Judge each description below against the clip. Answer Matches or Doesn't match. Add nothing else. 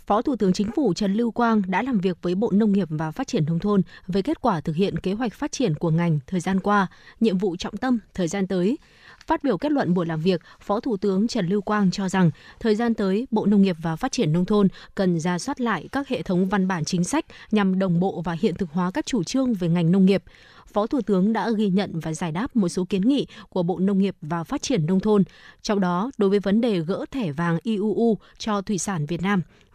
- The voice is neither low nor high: Doesn't match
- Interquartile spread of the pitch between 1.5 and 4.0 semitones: Matches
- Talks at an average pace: Doesn't match